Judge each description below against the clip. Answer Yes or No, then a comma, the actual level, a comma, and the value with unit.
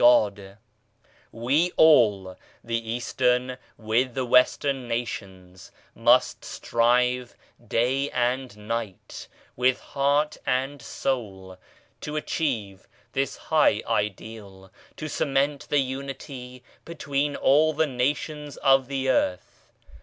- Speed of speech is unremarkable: No, slow, 110 wpm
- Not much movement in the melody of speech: No, average, 3.8 semitones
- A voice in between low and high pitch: No, low, 125 Hz